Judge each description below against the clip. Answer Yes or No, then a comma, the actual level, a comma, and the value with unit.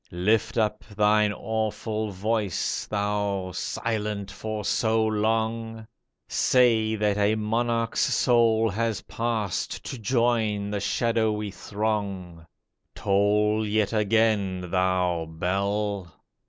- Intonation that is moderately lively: No, narrow, 1.8 semitones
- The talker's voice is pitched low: Yes, low, 105 Hz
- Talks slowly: Yes, slow, 100 wpm